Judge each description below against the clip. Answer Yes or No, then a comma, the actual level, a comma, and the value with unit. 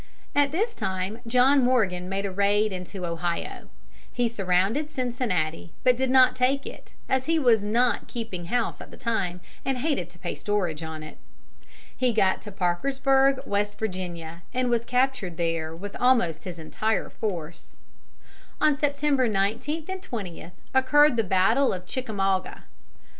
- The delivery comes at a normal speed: Yes, average, 155 wpm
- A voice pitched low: No, high, 220 Hz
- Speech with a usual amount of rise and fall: No, wide, 6.2 semitones